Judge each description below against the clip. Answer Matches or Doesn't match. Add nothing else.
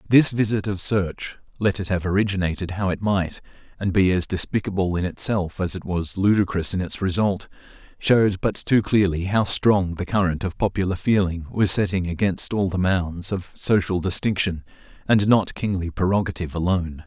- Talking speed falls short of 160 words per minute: Doesn't match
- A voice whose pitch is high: Doesn't match